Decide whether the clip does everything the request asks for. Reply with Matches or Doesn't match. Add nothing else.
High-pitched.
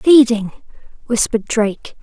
Matches